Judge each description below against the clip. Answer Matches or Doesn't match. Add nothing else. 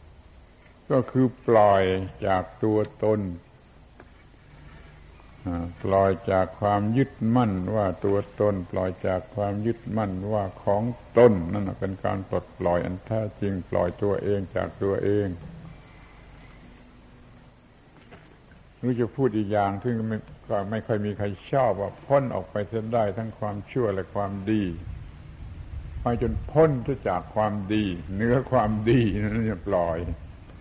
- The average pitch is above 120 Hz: Doesn't match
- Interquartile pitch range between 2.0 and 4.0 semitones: Matches